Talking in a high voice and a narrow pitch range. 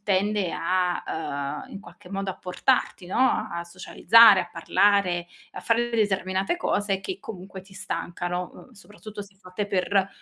Yes: high, 195 Hz; narrow, 2.2 semitones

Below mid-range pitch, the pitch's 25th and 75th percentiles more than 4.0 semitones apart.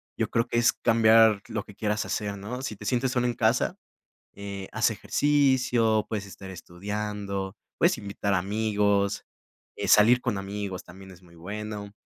No: low, 105 Hz; narrow, 2.4 semitones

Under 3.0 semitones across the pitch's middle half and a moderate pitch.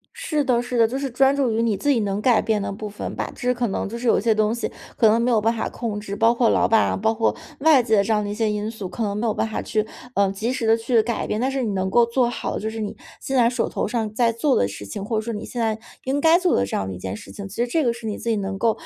No: narrow, 2.5 semitones; high, 225 Hz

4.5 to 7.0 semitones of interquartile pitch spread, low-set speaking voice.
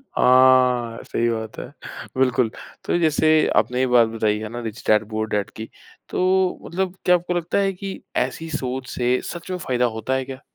Yes: wide, 5.6 semitones; low, 125 Hz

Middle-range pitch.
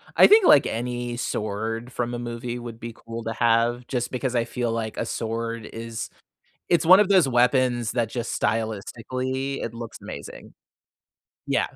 No: low, 120 Hz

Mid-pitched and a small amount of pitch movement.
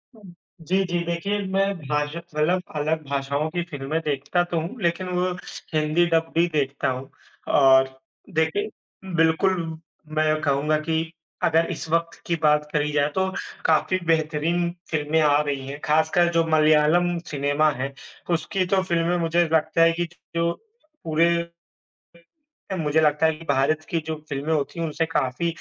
Yes: medium, 160 Hz; narrow, 2.2 semitones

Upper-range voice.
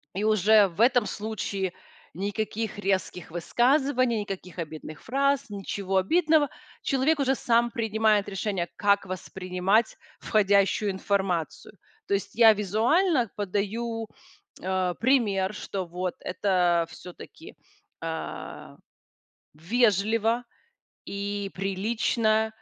Yes: high, 205 Hz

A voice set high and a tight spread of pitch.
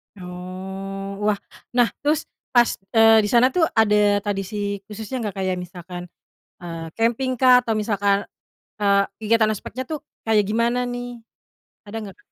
No: high, 210 Hz; average, 3.4 semitones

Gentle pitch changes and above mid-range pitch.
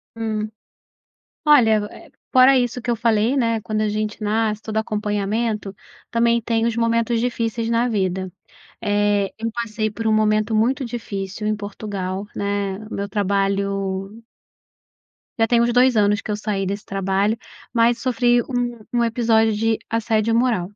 Yes: narrow, 2.2 semitones; high, 220 Hz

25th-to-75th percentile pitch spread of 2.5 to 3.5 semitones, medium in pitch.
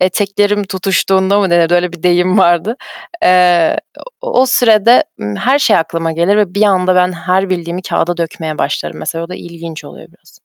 Yes: average, 2.8 semitones; medium, 180 Hz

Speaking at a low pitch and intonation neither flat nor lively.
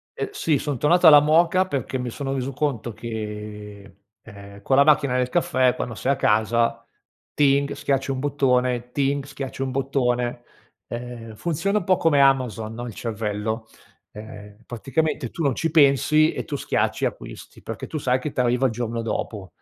Yes: low, 130 Hz; average, 3.9 semitones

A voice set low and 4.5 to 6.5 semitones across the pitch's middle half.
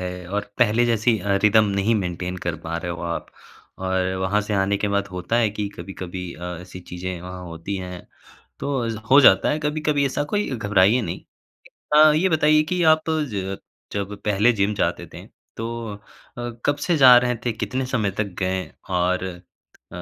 Yes: low, 100 Hz; average, 5.0 semitones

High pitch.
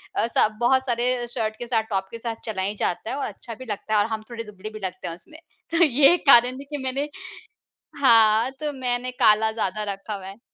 Yes: high, 230 Hz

